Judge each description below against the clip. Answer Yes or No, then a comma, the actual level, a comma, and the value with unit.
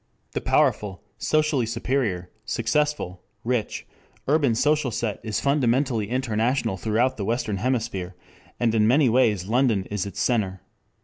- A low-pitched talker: Yes, low, 115 Hz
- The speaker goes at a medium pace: No, slow, 130 wpm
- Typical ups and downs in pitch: Yes, average, 3.8 semitones